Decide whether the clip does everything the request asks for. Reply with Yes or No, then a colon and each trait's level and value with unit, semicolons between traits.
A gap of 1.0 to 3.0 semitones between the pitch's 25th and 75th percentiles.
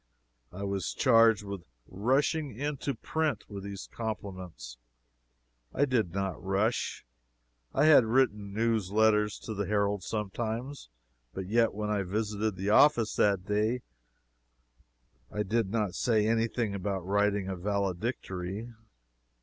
Yes: average, 2.7 semitones